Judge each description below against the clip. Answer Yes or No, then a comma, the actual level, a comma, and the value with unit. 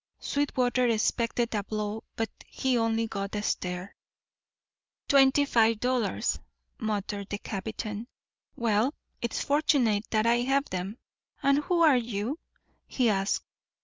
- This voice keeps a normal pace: No, slow, 125 wpm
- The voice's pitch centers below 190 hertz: No, high, 225 Hz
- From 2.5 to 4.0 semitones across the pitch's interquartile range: Yes, average, 3.6 semitones